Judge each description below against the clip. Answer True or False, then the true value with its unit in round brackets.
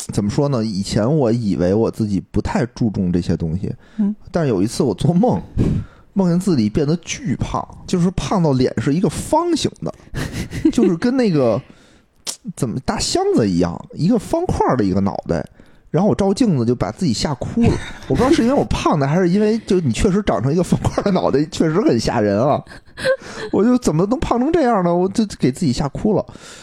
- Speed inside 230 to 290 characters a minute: False (300 characters per minute)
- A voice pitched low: False (180 Hz)